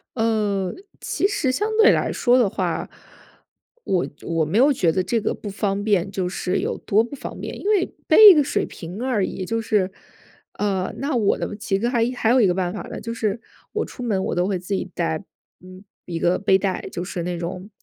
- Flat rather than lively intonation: No, average, 4.2 semitones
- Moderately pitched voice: No, high, 200 Hz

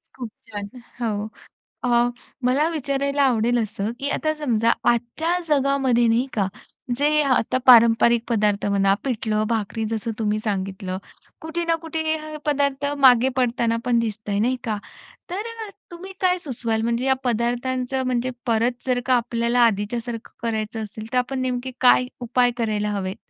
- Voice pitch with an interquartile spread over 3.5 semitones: No, average, 3.2 semitones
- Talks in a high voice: Yes, high, 240 Hz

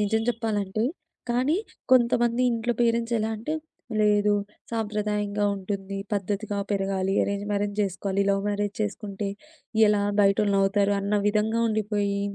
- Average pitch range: No, narrow, 1.8 semitones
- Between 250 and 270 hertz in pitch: No, high, 205 Hz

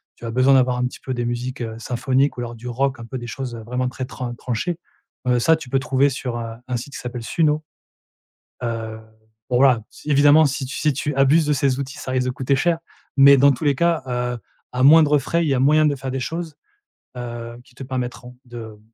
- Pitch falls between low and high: No, low, 130 Hz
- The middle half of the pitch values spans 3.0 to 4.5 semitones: No, narrow, 2.5 semitones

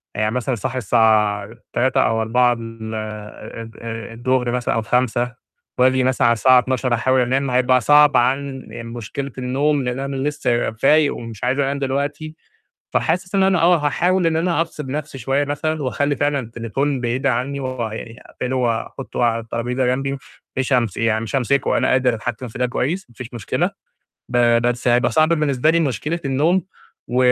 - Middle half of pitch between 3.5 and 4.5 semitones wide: No, average, 3.0 semitones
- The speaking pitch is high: No, low, 130 Hz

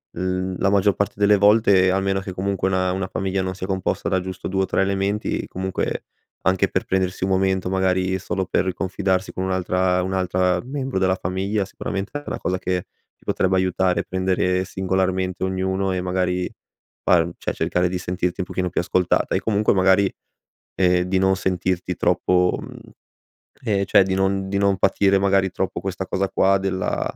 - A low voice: Yes, very low, 95 Hz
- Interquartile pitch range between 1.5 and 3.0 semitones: No, narrow, 0.9 semitones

